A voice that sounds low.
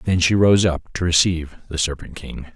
Yes: very low, 85 Hz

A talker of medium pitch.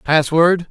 Yes: medium, 160 Hz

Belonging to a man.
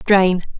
No: female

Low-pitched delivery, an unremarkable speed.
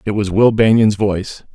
Yes: low, 105 Hz; average, 195 wpm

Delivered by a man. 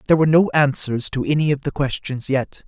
Yes: male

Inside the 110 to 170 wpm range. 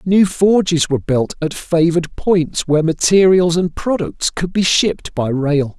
Yes: average, 165 wpm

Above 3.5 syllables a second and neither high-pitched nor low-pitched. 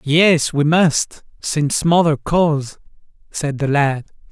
No: 3.3 syllables/s; medium, 150 Hz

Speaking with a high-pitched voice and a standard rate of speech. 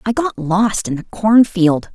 Yes: high, 200 Hz; average, 185 wpm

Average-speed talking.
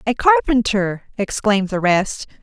No: slow, 125 wpm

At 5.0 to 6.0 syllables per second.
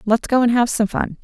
Yes: 5.5 syllables/s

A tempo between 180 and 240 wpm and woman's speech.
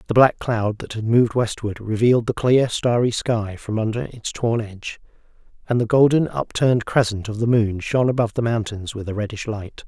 No: average, 200 wpm; male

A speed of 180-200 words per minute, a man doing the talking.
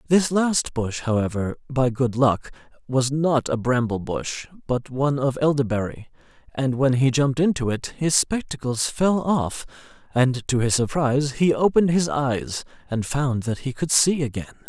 No: average, 170 wpm; male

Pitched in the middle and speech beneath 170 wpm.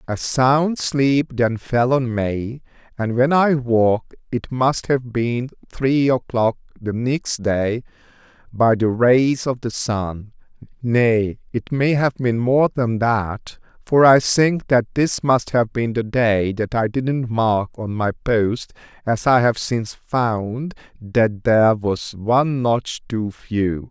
No: low, 120 Hz; average, 160 wpm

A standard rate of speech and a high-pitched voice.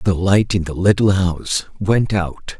No: average, 185 wpm; very low, 95 Hz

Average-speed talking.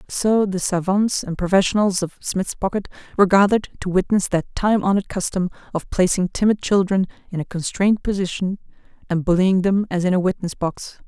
Yes: average, 175 wpm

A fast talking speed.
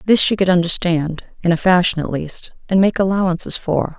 No: average, 195 wpm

